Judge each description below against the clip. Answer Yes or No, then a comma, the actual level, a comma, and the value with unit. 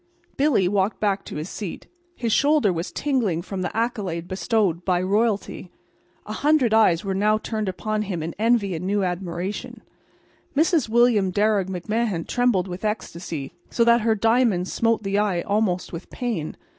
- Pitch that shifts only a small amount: No, average, 3.9 semitones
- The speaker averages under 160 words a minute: No, average, 165 wpm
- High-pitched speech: Yes, high, 205 Hz